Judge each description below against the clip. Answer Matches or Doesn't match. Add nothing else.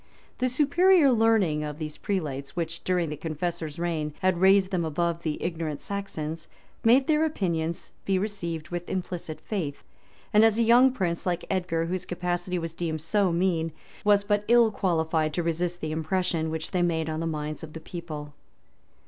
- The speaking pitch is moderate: Matches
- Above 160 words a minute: Matches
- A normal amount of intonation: Matches